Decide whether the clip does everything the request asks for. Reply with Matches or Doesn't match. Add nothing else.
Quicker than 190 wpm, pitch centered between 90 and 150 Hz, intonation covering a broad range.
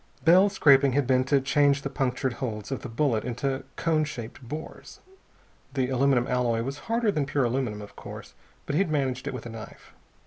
Doesn't match